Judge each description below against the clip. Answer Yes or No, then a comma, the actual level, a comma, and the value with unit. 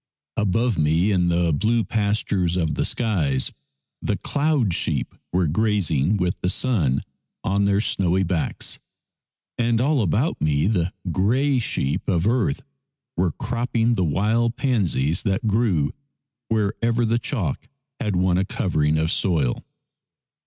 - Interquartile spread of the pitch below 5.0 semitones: No, average, 5.3 semitones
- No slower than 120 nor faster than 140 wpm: Yes, slow, 135 wpm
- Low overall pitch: Yes, low, 100 Hz